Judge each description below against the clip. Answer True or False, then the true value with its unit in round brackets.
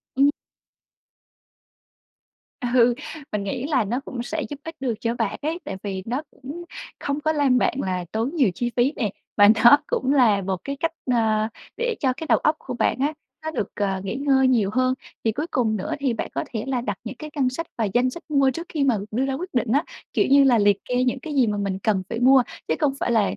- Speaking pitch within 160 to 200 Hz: False (255 Hz)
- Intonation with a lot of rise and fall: False (4.2 semitones)